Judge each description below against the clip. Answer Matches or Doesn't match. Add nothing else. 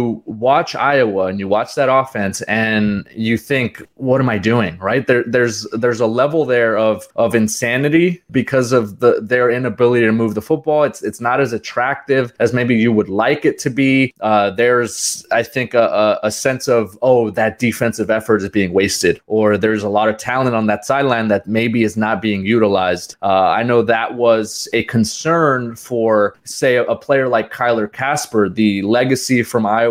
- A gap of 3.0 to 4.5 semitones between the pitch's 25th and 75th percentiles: Doesn't match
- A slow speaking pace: Doesn't match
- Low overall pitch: Matches